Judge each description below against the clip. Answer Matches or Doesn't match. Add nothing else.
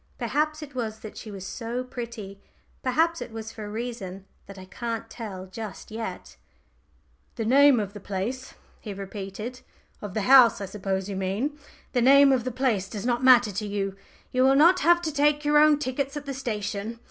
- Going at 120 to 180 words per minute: Doesn't match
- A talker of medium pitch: Doesn't match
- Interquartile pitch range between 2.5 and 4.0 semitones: Doesn't match